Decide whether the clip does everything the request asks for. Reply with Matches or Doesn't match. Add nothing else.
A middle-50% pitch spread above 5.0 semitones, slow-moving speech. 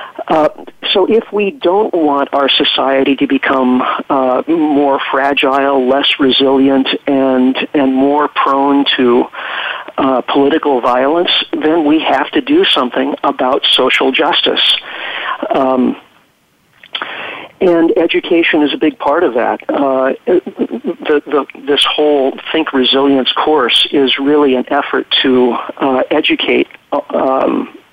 Doesn't match